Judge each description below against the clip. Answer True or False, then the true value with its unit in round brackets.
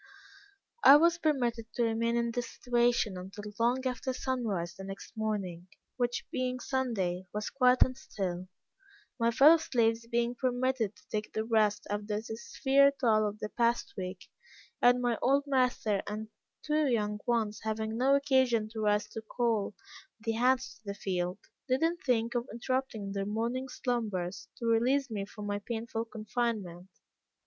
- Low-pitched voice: False (230 Hz)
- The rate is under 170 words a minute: True (160 wpm)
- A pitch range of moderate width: True (3.2 semitones)